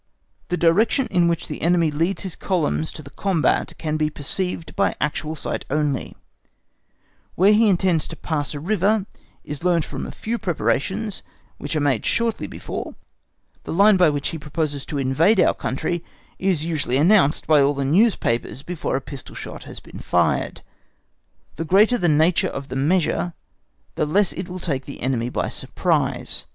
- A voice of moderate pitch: Yes, medium, 165 Hz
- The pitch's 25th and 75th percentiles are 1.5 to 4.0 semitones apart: No, average, 4.4 semitones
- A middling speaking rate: Yes, average, 175 wpm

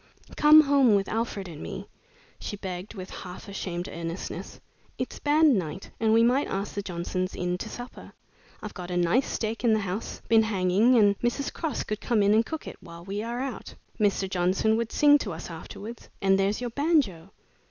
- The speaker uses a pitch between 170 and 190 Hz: No, high, 205 Hz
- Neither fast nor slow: Yes, average, 195 wpm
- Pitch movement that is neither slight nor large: Yes, average, 4.4 semitones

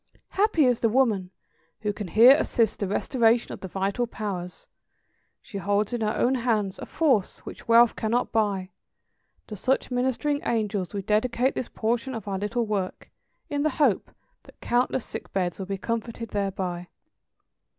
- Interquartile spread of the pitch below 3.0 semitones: No, average, 3.7 semitones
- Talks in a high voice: Yes, high, 220 Hz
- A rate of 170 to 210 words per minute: No, average, 160 wpm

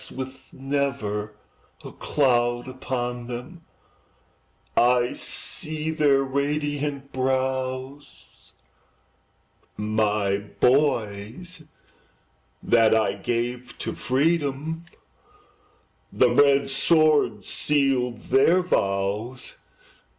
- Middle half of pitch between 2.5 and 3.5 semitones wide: Yes, average, 3.2 semitones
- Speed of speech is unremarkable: No, slow, 70 wpm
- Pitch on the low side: Yes, low, 130 Hz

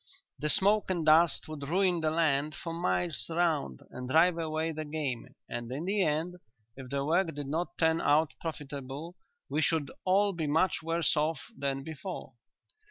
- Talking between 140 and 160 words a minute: No, average, 170 wpm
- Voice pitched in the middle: Yes, medium, 160 Hz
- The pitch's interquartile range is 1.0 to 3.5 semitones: Yes, average, 2.8 semitones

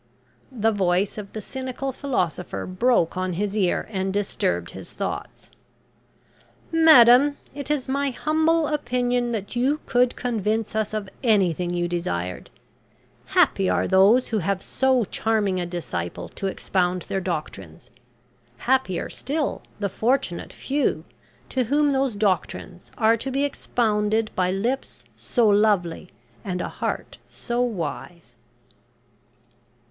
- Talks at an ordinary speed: No, slow, 130 wpm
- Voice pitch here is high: Yes, high, 215 Hz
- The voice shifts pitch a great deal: Yes, wide, 5.7 semitones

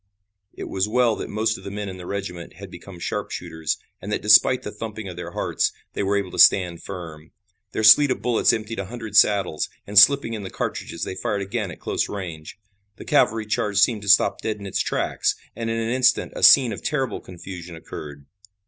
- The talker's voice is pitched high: No, low, 100 Hz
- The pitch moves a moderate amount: Yes, average, 3.3 semitones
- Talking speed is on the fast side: Yes, fast, 215 wpm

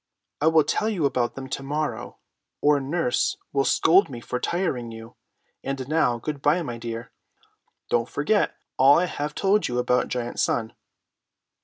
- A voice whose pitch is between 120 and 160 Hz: Yes, medium, 140 Hz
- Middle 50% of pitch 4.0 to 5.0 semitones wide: Yes, average, 4.5 semitones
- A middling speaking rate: Yes, average, 165 wpm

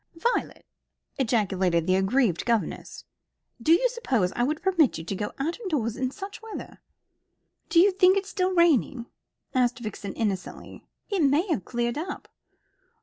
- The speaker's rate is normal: Yes, average, 155 wpm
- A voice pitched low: No, very high, 265 Hz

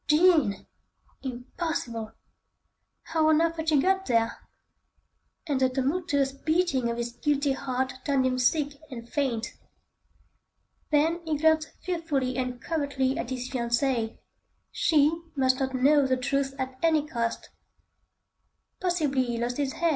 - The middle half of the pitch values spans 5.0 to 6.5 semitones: No, average, 3.7 semitones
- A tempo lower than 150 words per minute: Yes, slow, 135 wpm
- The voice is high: Yes, very high, 275 Hz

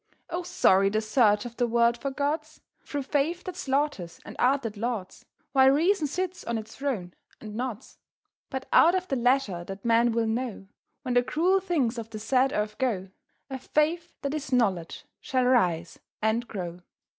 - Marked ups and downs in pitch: No, average, 4.7 semitones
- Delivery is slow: No, average, 180 wpm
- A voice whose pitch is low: No, high, 245 Hz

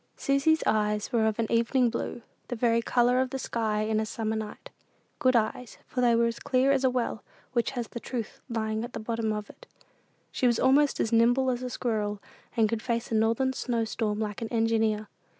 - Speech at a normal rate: No, fast, 215 wpm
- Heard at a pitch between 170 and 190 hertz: No, high, 230 Hz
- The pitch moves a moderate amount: No, narrow, 2.3 semitones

